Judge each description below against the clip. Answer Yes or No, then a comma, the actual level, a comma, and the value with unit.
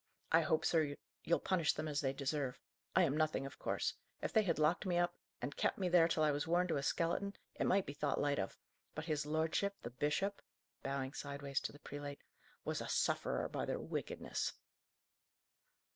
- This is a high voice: No, medium, 155 Hz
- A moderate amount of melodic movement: Yes, average, 3.2 semitones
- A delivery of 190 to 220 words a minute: Yes, average, 200 wpm